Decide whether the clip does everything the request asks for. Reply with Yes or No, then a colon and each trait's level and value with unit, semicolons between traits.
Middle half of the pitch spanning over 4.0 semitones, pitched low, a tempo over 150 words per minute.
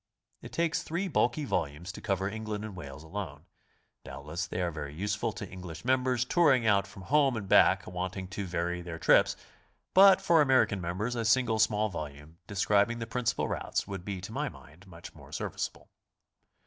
Yes: average, 5.2 semitones; low, 100 Hz; average, 185 wpm